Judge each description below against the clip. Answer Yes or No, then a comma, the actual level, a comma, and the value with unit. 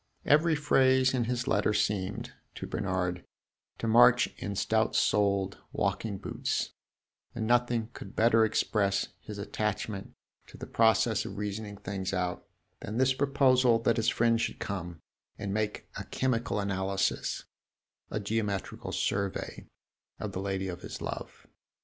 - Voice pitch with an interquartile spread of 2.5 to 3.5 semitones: Yes, average, 3.0 semitones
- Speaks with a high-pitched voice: No, low, 105 Hz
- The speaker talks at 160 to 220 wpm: No, average, 140 wpm